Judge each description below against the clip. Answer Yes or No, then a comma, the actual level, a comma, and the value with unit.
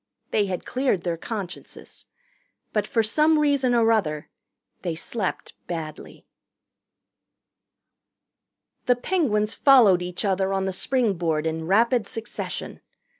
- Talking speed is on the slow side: Yes, slow, 115 wpm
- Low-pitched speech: No, high, 210 Hz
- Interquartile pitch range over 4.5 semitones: Yes, wide, 5.4 semitones